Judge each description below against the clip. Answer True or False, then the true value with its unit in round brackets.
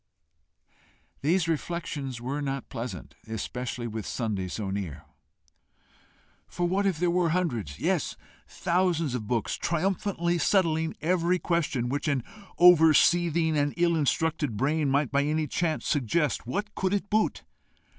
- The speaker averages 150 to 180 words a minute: False (135 wpm)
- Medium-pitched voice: True (155 Hz)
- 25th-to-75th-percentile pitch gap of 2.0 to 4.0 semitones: False (5.3 semitones)